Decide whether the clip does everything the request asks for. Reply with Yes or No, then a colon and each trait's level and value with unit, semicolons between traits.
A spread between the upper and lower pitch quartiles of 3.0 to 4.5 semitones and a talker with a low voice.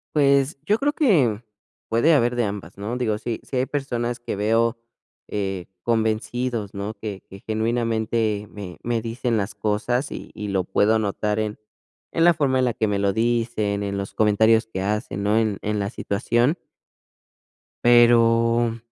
No: narrow, 2.6 semitones; low, 115 Hz